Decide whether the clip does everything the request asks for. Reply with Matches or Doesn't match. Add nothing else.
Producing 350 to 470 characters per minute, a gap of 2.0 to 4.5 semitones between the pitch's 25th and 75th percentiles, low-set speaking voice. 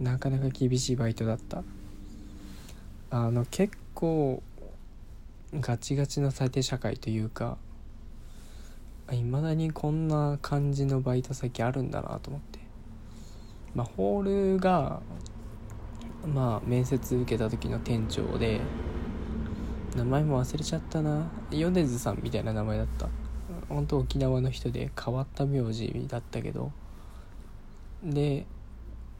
Doesn't match